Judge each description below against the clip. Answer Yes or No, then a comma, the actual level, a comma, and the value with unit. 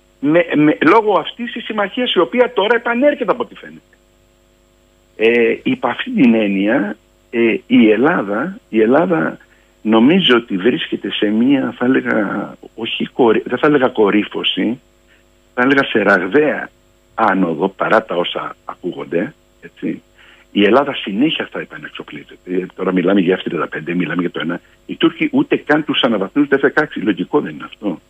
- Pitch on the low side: Yes, low, 120 Hz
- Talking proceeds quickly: No, average, 150 wpm